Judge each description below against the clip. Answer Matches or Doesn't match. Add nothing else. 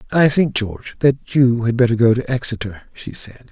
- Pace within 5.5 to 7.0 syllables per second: Doesn't match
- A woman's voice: Doesn't match